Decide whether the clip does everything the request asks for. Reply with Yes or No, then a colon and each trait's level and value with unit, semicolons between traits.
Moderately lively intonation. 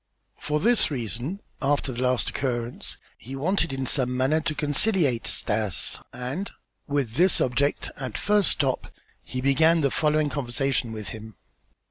Yes: average, 3.7 semitones